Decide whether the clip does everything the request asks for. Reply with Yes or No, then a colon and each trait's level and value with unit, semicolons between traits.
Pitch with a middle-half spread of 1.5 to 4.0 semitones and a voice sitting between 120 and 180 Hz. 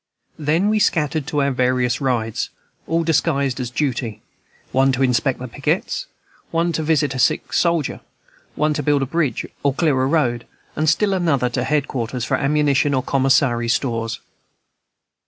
Yes: average, 3.6 semitones; medium, 140 Hz